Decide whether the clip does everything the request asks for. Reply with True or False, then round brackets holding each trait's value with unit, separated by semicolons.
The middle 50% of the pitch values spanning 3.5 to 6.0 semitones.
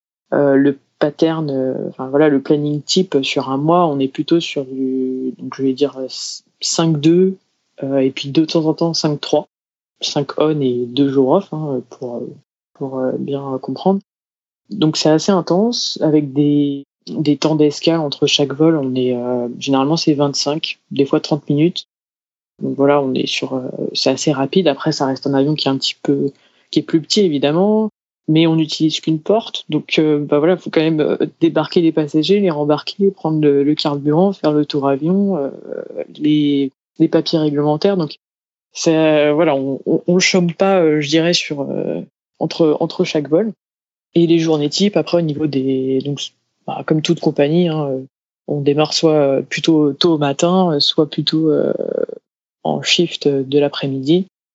False (3.0 semitones)